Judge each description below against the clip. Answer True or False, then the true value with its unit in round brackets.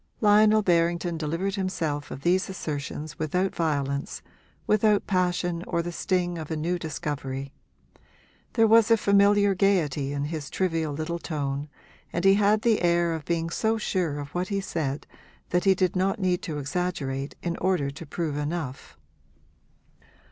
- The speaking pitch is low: False (170 Hz)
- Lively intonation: False (4.3 semitones)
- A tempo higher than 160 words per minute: False (155 wpm)